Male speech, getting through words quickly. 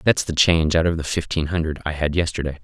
Yes: male; fast, 250 wpm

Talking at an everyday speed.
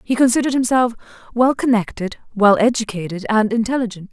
No: slow, 130 wpm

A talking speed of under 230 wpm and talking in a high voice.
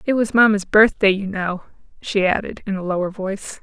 Yes: average, 200 wpm; high, 200 Hz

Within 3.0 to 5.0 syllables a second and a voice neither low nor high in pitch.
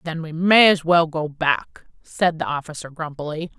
Yes: 4.7 syllables/s; medium, 160 Hz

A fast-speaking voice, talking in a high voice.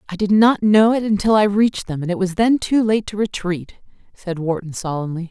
Yes: fast, 225 wpm; high, 195 Hz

